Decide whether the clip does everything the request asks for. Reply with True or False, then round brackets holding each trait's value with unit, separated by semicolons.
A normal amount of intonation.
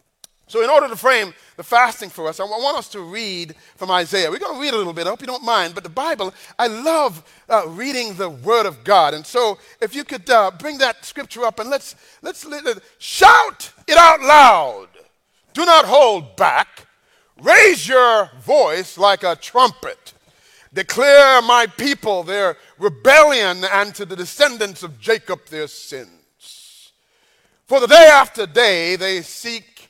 False (6.9 semitones)